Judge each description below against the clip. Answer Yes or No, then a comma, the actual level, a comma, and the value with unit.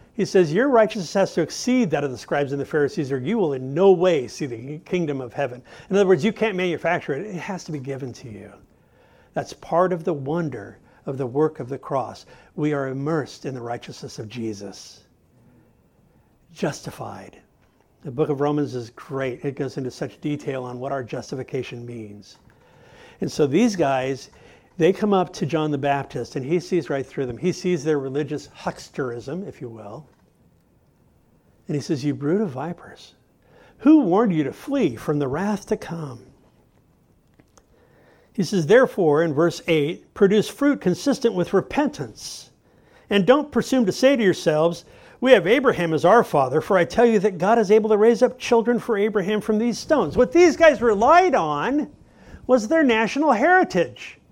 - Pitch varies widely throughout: Yes, wide, 7.4 semitones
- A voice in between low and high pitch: Yes, medium, 165 Hz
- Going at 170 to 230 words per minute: Yes, average, 185 wpm